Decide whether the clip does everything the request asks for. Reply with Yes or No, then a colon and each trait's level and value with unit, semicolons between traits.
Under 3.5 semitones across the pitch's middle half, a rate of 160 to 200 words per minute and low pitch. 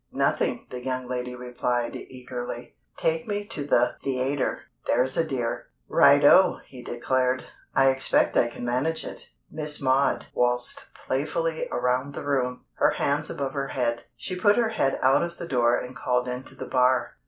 Yes: narrow, 2.4 semitones; average, 165 wpm; low, 130 Hz